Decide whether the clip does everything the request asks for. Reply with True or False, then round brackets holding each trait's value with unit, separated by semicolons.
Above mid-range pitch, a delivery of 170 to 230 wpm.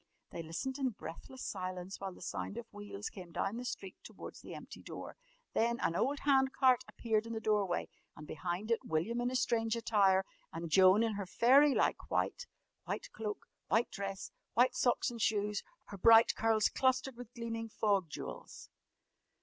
True (220 Hz; 180 wpm)